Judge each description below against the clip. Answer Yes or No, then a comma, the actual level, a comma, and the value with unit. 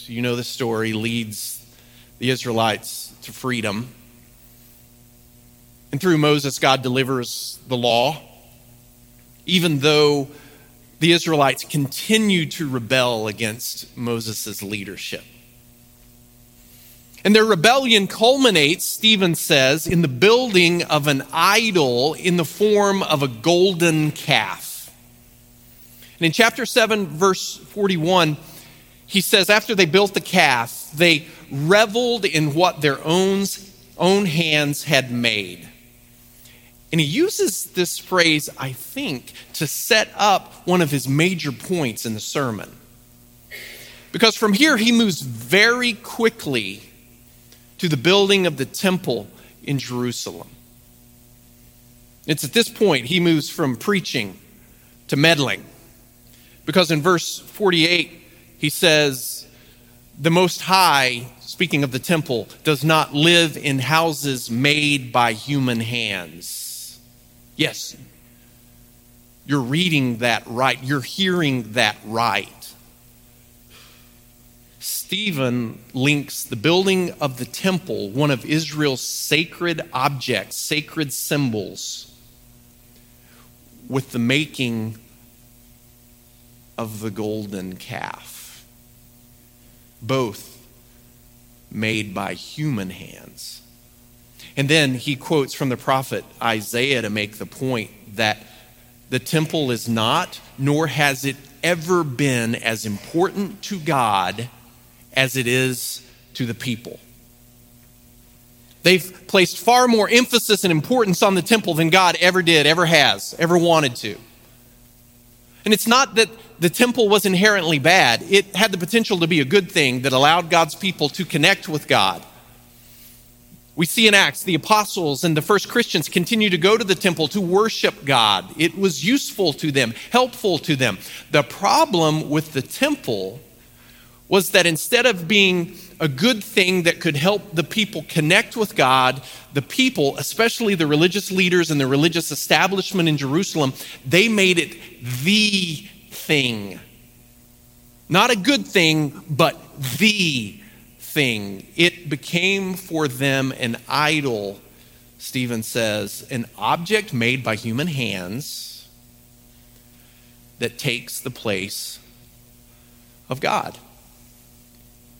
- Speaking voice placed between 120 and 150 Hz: Yes, low, 135 Hz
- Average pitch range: No, wide, 6.3 semitones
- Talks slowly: Yes, slow, 120 wpm